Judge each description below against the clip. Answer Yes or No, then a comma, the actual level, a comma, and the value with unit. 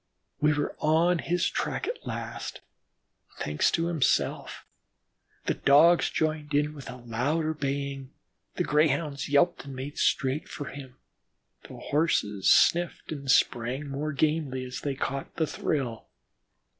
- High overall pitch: No, medium, 145 Hz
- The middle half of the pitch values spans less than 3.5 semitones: Yes, average, 2.7 semitones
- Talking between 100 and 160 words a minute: Yes, average, 140 wpm